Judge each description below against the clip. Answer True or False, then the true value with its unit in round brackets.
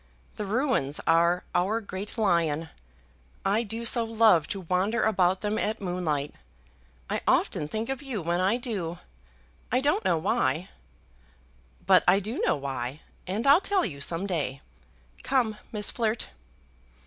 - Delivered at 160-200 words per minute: False (150 wpm)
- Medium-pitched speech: False (195 Hz)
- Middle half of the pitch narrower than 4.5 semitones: False (5.1 semitones)